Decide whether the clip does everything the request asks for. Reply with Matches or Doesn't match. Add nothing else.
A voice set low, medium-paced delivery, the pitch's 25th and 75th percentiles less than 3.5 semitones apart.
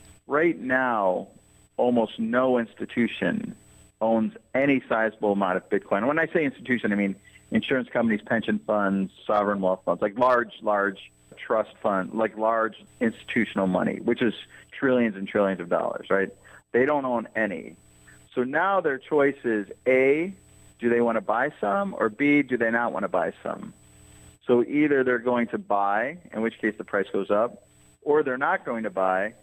Doesn't match